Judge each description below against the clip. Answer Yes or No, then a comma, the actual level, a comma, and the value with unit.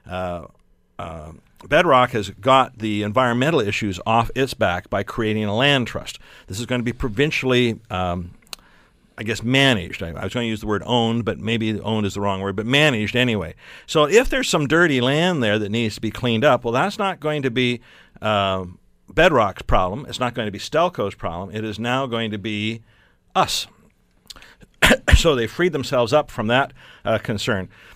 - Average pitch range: Yes, average, 3.9 semitones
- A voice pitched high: No, low, 115 Hz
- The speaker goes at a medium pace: Yes, average, 195 wpm